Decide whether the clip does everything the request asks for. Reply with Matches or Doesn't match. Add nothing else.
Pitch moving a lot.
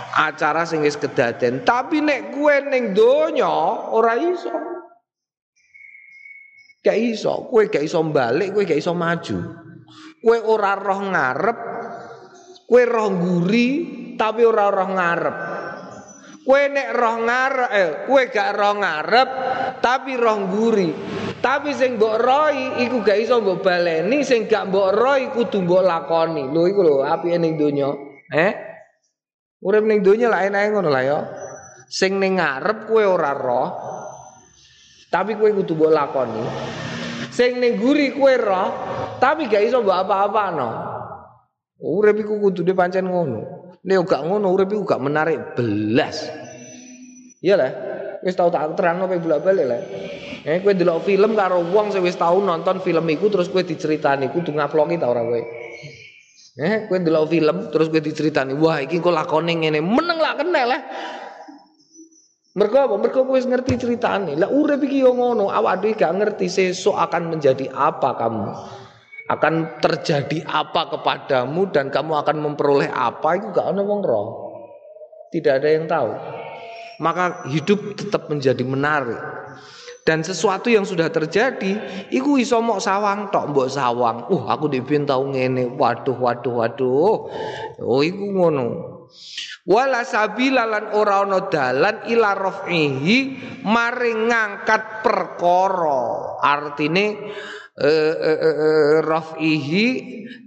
Matches